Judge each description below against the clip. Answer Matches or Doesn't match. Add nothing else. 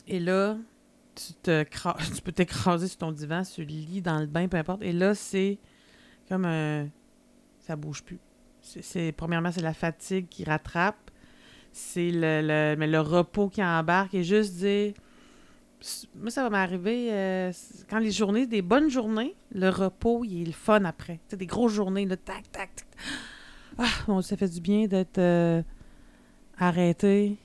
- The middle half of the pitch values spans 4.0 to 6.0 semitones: Doesn't match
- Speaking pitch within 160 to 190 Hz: Matches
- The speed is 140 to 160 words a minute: Doesn't match